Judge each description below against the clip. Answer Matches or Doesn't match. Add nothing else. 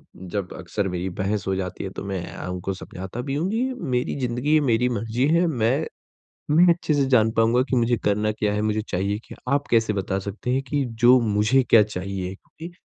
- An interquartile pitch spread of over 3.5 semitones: Matches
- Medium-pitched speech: Doesn't match